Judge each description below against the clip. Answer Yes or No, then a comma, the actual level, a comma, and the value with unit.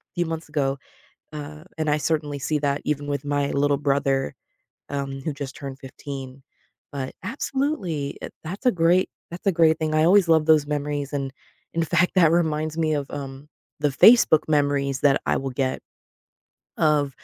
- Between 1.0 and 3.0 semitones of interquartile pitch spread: Yes, narrow, 2.4 semitones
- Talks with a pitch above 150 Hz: No, medium, 145 Hz